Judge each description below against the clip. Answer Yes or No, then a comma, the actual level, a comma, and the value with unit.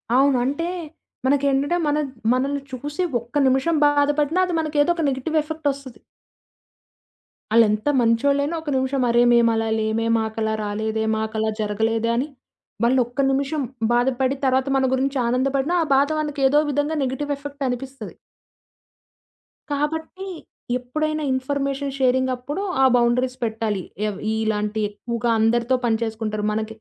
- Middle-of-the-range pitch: No, very high, 260 Hz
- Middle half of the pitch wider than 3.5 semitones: Yes, average, 4.0 semitones